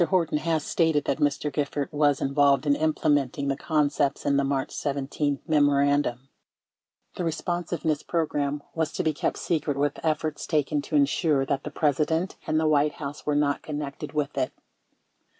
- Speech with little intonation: Yes, narrow, 1.7 semitones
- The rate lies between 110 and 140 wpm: No, average, 165 wpm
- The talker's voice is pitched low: No, medium, 145 Hz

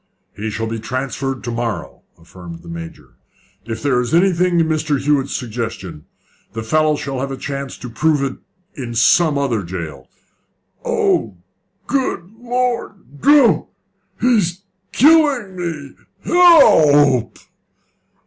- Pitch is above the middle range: No, medium, 140 Hz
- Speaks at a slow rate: Yes, slow, 130 wpm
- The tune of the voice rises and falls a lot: Yes, wide, 7.3 semitones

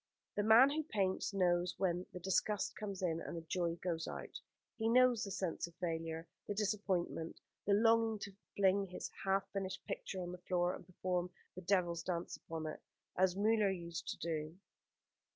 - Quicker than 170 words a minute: Yes, average, 180 wpm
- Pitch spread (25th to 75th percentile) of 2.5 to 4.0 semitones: Yes, average, 2.8 semitones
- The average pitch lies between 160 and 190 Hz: Yes, medium, 185 Hz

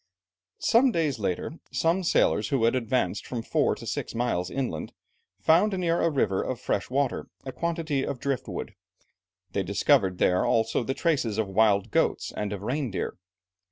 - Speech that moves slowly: No, average, 165 wpm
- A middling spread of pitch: No, wide, 7.1 semitones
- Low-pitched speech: Yes, low, 130 Hz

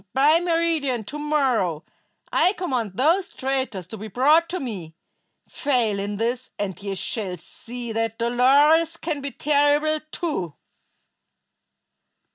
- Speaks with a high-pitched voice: Yes, very high, 260 Hz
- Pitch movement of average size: No, wide, 5.8 semitones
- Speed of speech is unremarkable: No, slow, 125 wpm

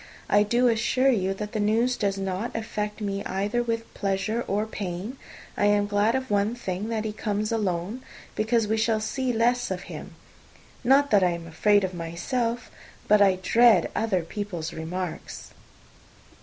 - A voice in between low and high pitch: No, high, 210 Hz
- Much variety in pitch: No, average, 3.1 semitones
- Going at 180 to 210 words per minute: No, average, 170 wpm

